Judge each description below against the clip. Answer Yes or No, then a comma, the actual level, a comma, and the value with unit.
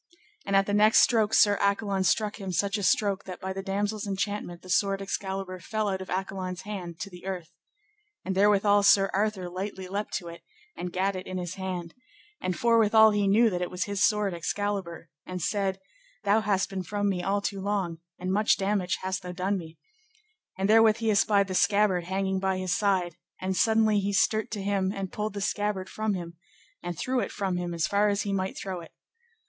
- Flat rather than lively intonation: Yes, narrow, 1.8 semitones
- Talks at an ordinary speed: No, fast, 210 wpm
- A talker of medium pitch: No, high, 195 Hz